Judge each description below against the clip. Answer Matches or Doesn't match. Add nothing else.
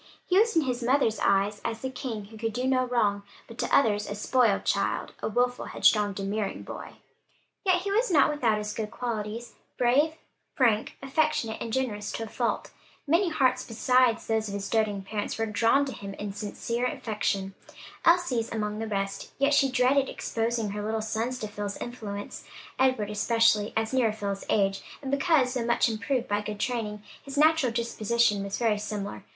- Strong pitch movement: Doesn't match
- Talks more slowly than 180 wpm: Doesn't match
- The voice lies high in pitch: Matches